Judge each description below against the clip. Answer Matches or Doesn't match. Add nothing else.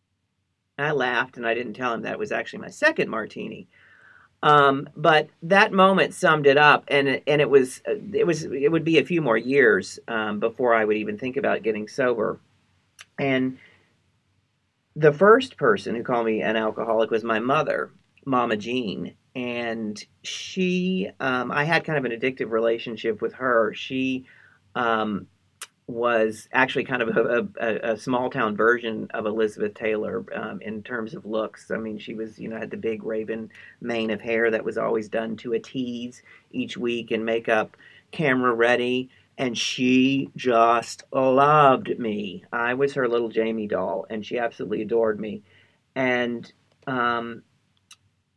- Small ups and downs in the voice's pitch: Doesn't match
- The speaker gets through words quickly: Doesn't match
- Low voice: Matches